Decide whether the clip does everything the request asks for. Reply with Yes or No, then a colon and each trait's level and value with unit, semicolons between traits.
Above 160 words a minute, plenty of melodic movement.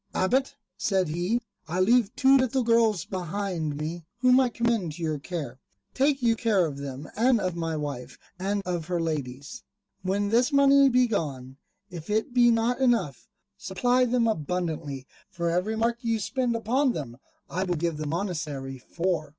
Yes: average, 175 wpm; wide, 7.0 semitones